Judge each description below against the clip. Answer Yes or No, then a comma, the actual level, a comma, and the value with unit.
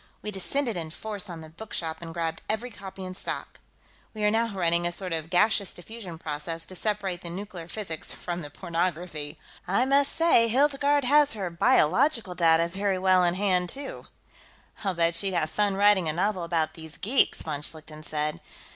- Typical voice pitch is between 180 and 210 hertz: Yes, medium, 185 Hz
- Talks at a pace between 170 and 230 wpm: Yes, average, 185 wpm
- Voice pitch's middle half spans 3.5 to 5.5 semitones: Yes, average, 4.1 semitones